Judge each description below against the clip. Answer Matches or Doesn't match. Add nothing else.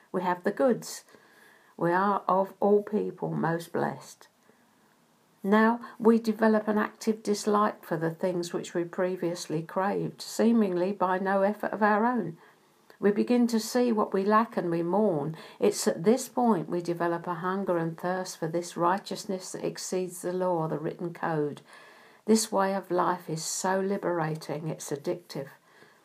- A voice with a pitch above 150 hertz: Matches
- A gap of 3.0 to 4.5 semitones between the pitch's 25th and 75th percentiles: Matches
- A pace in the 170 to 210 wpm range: Doesn't match